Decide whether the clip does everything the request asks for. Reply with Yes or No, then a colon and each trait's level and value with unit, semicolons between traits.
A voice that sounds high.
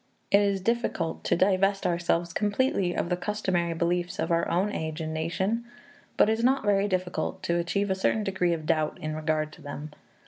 No: medium, 180 Hz